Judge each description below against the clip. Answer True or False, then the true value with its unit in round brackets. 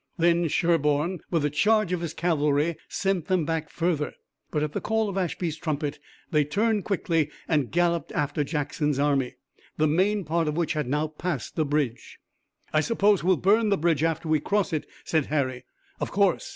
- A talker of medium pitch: True (160 Hz)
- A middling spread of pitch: True (3.4 semitones)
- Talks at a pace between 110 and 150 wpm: False (185 wpm)